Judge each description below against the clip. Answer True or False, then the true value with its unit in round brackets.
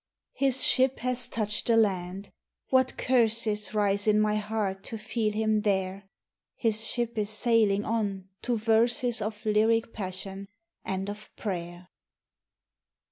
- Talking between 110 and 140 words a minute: True (135 wpm)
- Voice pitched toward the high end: True (215 Hz)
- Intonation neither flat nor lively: False (2.3 semitones)